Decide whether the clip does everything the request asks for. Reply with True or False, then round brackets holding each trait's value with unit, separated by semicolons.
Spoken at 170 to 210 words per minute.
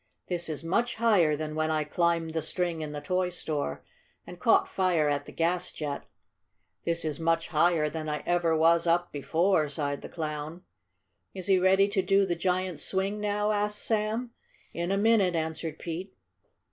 True (180 wpm)